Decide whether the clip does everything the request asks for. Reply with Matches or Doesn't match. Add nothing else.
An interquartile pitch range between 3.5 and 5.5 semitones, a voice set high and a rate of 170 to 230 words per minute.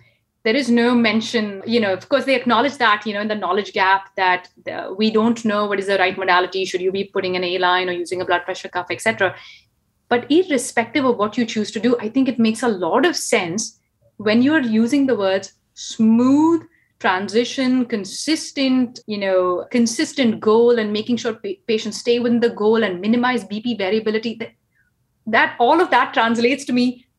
Matches